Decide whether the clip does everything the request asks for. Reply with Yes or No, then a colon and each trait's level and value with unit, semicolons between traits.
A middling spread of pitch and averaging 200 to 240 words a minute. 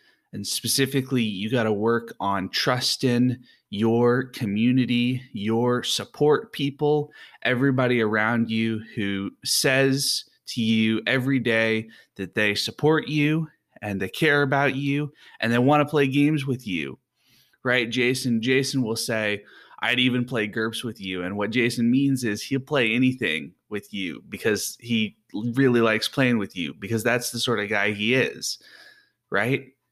No: average, 3.3 semitones; average, 150 wpm